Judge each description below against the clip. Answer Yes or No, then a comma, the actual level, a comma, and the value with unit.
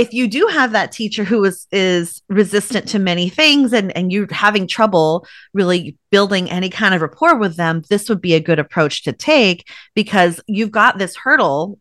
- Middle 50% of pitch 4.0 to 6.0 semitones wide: No, average, 3.6 semitones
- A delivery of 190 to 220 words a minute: Yes, average, 200 wpm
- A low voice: No, high, 200 Hz